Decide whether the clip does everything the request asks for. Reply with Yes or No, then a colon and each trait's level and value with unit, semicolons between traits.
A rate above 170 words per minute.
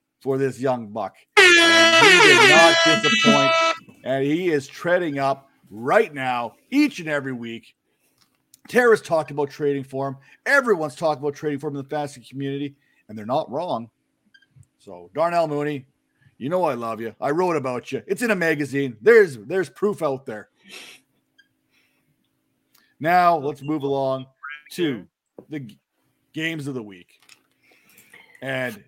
No: average, 150 wpm